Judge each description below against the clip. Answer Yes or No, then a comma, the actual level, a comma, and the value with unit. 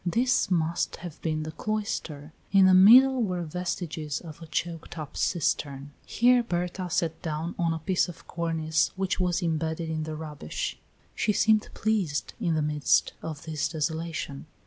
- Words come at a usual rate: Yes, average, 165 wpm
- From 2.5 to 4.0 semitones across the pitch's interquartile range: Yes, average, 2.9 semitones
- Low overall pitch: No, medium, 165 Hz